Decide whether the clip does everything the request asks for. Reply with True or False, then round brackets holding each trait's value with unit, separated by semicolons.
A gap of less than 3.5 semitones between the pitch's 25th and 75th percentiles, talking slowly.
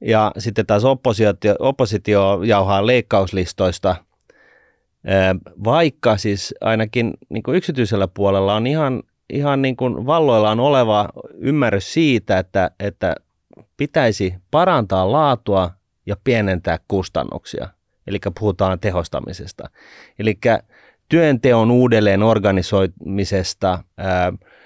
False (3.8 semitones; 90 wpm)